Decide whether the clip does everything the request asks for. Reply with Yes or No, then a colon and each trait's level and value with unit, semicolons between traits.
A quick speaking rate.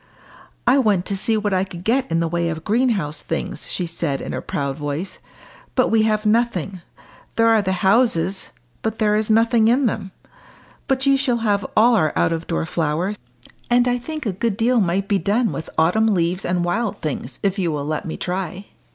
Yes: fast, 210 wpm